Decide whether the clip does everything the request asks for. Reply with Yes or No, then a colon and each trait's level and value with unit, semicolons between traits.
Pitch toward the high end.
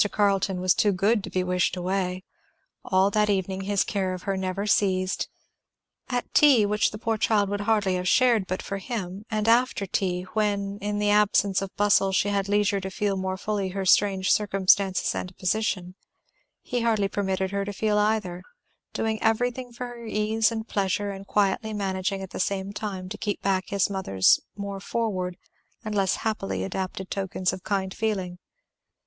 Yes: high, 200 Hz